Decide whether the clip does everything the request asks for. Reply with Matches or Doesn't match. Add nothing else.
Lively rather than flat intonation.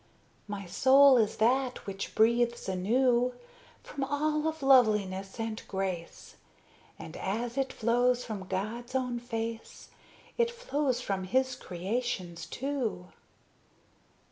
Doesn't match